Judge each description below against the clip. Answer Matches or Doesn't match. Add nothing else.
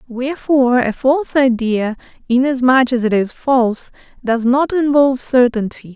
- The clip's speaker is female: Matches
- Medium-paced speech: Doesn't match